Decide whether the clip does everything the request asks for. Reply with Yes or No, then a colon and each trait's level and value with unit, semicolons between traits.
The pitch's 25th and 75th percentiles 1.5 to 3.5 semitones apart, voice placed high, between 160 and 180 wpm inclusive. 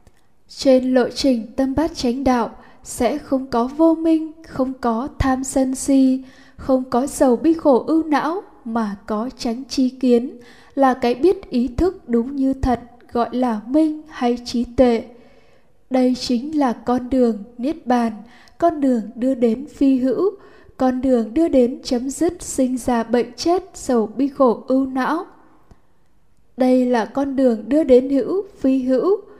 Yes: average, 2.8 semitones; very high, 260 Hz; slow, 165 wpm